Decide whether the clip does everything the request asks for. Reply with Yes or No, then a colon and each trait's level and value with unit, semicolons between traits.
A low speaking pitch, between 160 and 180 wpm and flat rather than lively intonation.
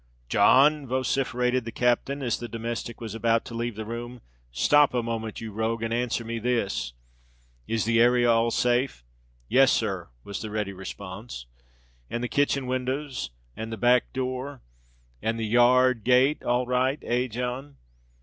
No: low, 120 Hz; average, 150 wpm; narrow, 2.3 semitones